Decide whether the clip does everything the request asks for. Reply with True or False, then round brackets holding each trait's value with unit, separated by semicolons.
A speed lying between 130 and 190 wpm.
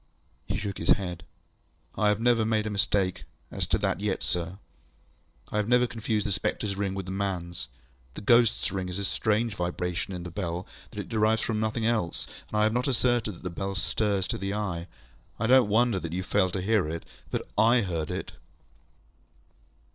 False (200 wpm)